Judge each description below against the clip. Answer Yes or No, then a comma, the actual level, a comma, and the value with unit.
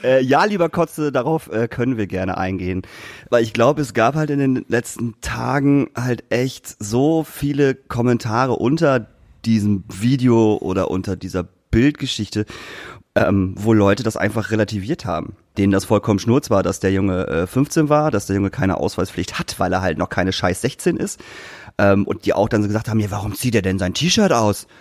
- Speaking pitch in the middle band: No, low, 110 Hz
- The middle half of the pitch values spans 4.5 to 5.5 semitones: Yes, average, 4.9 semitones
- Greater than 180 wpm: Yes, fast, 190 wpm